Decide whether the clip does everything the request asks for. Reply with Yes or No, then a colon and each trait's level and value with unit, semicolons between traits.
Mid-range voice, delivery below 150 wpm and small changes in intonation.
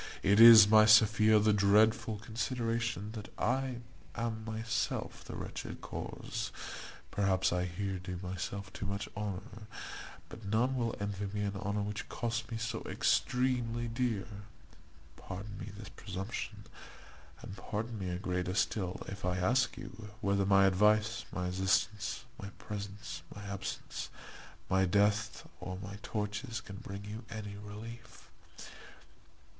No: low, 105 Hz; average, 140 wpm; narrow, 2.3 semitones